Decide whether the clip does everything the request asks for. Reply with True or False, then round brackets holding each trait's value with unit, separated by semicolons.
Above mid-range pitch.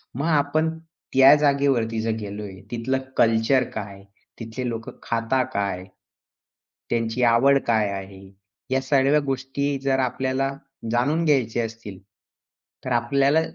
False (125 Hz)